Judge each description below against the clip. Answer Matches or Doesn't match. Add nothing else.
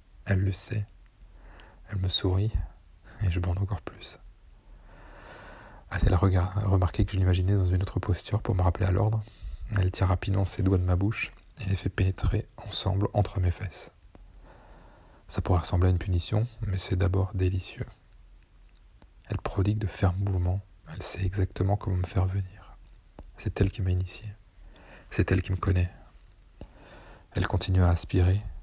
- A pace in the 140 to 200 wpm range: Matches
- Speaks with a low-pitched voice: Matches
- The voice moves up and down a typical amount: Doesn't match